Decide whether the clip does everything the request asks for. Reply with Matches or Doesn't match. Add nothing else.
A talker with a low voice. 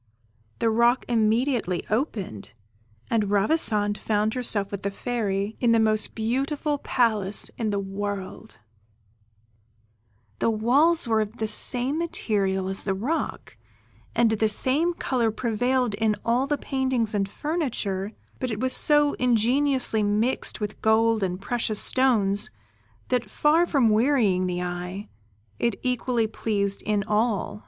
Doesn't match